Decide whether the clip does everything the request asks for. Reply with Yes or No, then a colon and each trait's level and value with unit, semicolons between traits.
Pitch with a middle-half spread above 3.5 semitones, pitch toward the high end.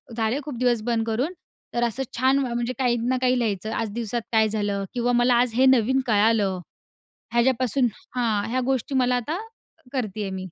No: average, 2.7 semitones; high, 240 Hz